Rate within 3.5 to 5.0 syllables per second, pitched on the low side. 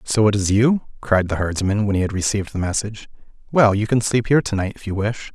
No: 6.2 syllables/s; low, 105 Hz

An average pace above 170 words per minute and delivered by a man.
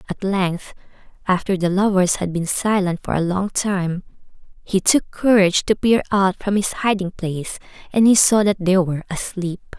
No: average, 180 wpm; female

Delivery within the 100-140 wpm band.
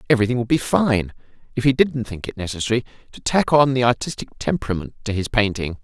No: average, 195 wpm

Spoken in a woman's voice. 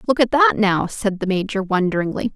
Yes: female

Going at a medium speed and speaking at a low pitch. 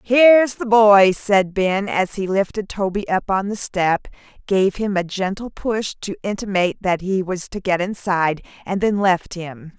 No: average, 185 wpm; high, 195 Hz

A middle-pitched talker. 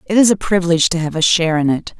Yes: medium, 175 Hz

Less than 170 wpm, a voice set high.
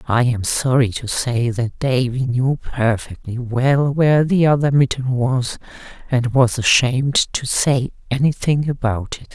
No: average, 150 wpm; low, 130 Hz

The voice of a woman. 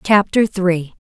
Yes: female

